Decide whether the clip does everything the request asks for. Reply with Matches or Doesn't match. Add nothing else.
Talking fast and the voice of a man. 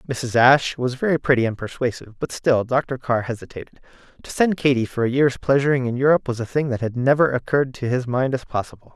Matches